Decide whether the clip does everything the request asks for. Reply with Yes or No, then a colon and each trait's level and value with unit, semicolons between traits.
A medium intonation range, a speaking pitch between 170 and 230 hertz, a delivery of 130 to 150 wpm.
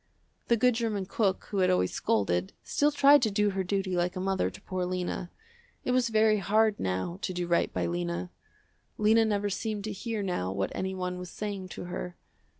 No: average, 3.4 semitones; high, 190 Hz; average, 200 wpm